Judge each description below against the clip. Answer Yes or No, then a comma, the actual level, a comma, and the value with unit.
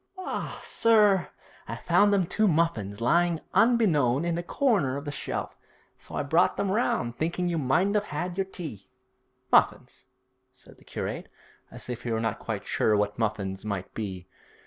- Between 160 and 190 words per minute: Yes, average, 170 wpm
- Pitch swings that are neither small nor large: No, wide, 9.0 semitones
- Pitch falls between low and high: Yes, medium, 160 Hz